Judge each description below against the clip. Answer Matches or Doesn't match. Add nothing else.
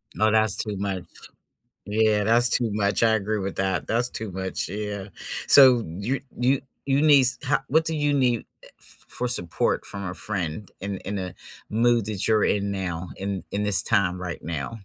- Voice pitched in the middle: Doesn't match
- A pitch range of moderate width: Matches